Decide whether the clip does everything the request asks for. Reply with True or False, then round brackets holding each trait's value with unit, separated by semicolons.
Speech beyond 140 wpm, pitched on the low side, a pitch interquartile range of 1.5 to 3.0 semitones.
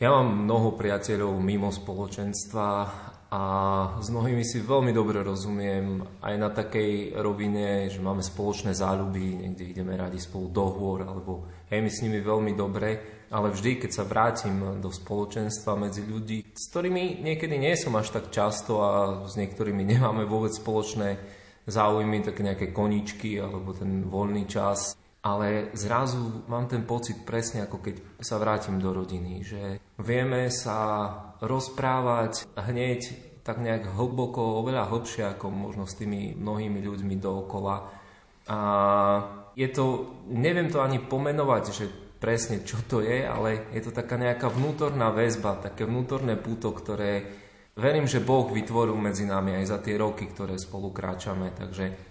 True (150 wpm; 105 Hz; 2.6 semitones)